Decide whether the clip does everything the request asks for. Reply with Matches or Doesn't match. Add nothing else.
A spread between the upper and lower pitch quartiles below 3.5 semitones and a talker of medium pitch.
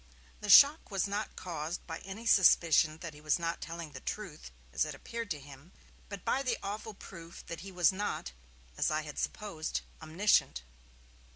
Doesn't match